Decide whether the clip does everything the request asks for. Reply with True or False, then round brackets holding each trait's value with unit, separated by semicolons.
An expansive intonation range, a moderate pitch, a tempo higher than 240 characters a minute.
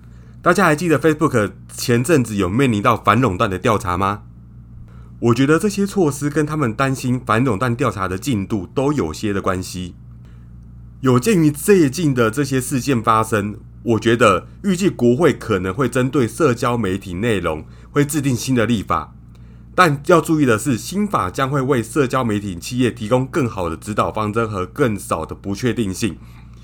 False (6.8 semitones; 115 Hz; 280 characters per minute)